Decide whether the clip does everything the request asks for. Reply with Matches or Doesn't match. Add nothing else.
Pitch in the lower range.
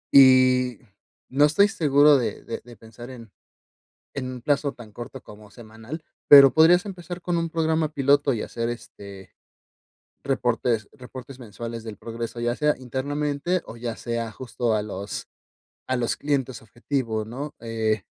Matches